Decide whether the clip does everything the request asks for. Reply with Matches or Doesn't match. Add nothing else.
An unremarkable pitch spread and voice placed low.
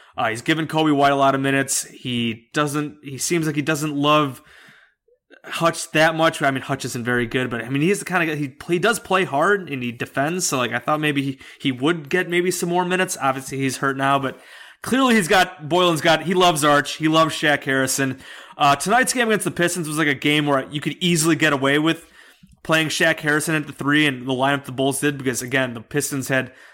Doesn't match